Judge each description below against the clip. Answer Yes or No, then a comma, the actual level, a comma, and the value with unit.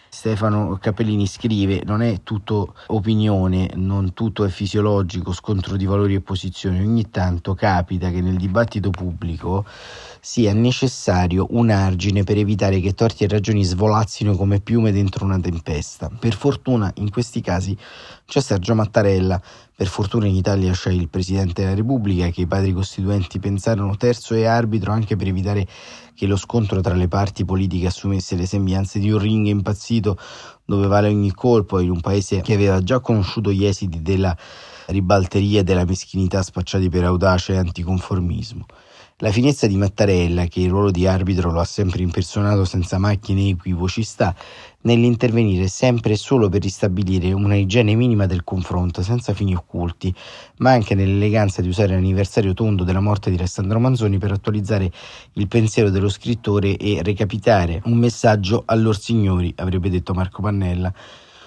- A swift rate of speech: No, average, 160 wpm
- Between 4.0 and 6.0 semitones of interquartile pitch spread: No, narrow, 2.5 semitones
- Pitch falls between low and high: No, low, 100 Hz